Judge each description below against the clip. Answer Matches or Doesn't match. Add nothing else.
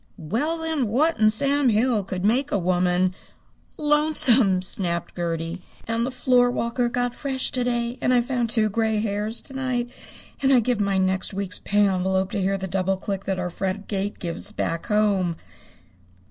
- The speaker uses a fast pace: Doesn't match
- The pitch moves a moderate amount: Matches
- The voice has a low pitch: Doesn't match